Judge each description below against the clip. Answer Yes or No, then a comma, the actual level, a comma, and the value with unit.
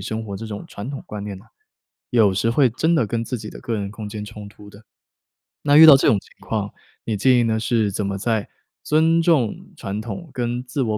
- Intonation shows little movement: No, average, 3.3 semitones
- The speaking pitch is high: No, low, 110 Hz